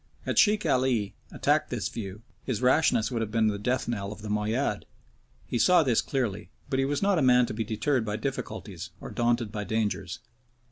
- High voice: No, low, 115 Hz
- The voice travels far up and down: No, average, 3.6 semitones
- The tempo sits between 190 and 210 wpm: Yes, average, 200 wpm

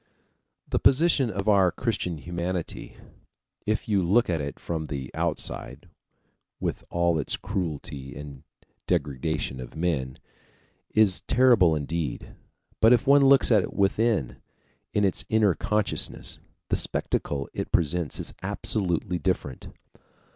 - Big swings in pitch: Yes, wide, 6.3 semitones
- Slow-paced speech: Yes, slow, 125 wpm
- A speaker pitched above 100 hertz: No, very low, 90 Hz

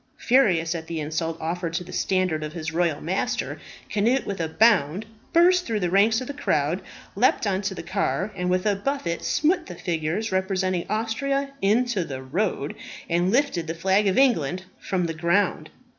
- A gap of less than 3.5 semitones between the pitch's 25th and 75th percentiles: No, average, 4.6 semitones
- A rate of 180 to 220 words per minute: Yes, average, 185 wpm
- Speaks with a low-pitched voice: No, medium, 185 Hz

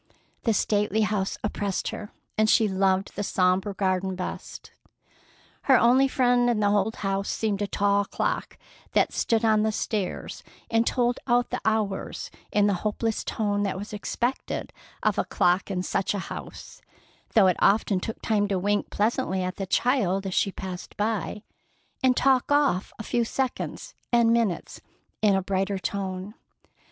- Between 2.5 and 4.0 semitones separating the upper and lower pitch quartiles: Yes, average, 2.8 semitones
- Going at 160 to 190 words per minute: Yes, average, 165 wpm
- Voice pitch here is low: No, high, 205 Hz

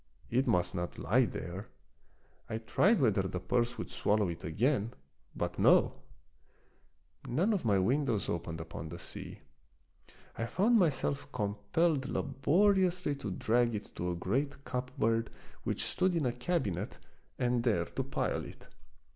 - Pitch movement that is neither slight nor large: No, wide, 6.4 semitones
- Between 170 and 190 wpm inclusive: No, average, 150 wpm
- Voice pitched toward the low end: Yes, low, 120 Hz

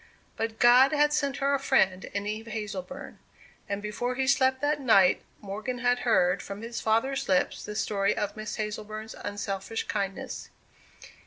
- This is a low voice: No, high, 220 Hz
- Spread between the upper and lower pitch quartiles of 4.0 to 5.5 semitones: Yes, average, 4.3 semitones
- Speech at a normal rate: Yes, average, 160 wpm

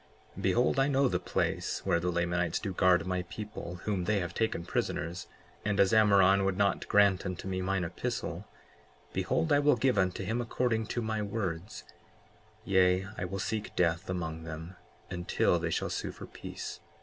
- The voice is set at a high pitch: No, very low, 95 Hz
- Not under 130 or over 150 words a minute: No, average, 180 wpm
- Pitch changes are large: No, average, 3.4 semitones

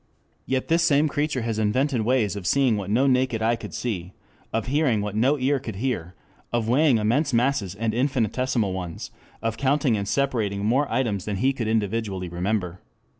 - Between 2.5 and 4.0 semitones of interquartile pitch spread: No, average, 4.4 semitones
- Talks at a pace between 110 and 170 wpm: No, average, 180 wpm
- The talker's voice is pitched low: Yes, low, 115 Hz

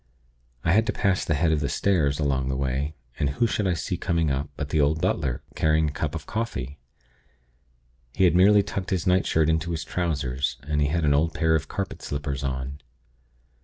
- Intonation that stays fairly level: No, average, 3.6 semitones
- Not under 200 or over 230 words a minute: Yes, fast, 205 wpm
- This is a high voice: No, very low, 80 Hz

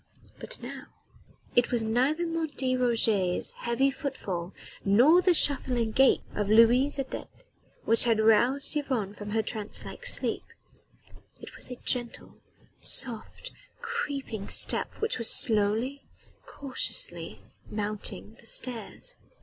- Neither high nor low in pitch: No, high, 240 Hz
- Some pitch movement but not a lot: Yes, average, 4.1 semitones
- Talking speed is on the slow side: Yes, slow, 120 wpm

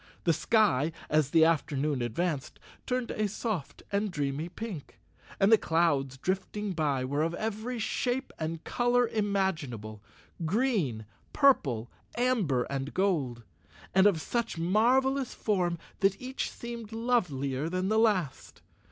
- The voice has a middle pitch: Yes, medium, 180 Hz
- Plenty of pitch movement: Yes, wide, 7.7 semitones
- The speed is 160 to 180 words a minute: No, slow, 135 wpm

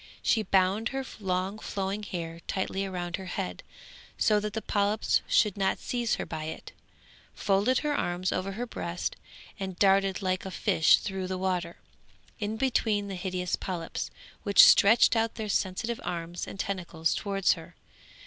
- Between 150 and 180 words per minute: Yes, average, 160 wpm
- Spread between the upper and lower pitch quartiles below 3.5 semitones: Yes, narrow, 2.5 semitones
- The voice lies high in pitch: Yes, high, 195 Hz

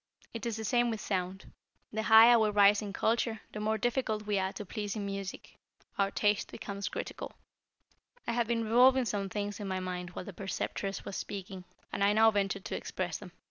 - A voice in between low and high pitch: No, high, 205 Hz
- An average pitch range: No, narrow, 2.1 semitones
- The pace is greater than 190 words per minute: Yes, fast, 205 wpm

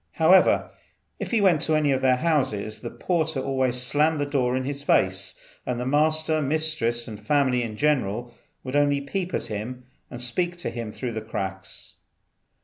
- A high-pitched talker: No, low, 130 Hz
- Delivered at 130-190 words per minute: Yes, average, 175 wpm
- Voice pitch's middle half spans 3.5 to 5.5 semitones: Yes, average, 4.4 semitones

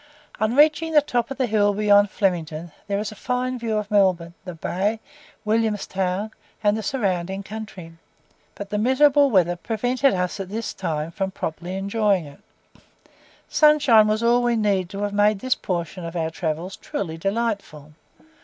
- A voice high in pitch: Yes, high, 205 Hz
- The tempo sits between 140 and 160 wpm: No, average, 170 wpm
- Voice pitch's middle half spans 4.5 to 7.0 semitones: No, average, 3.9 semitones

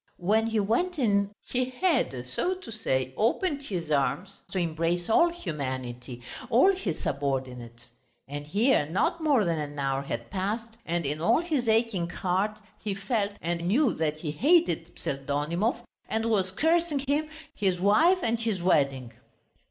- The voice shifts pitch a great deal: Yes, wide, 8.2 semitones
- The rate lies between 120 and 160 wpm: Yes, average, 155 wpm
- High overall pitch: Yes, high, 195 Hz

